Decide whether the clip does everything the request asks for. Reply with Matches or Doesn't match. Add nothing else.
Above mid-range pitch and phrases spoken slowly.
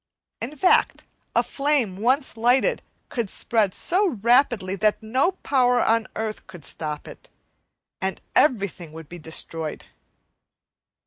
Matches